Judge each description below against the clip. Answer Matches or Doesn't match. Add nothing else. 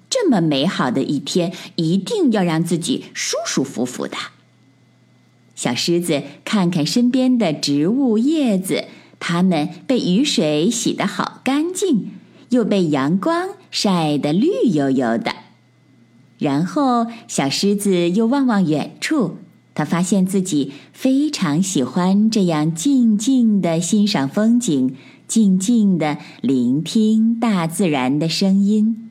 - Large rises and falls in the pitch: Matches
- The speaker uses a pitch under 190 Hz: Doesn't match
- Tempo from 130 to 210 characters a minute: Matches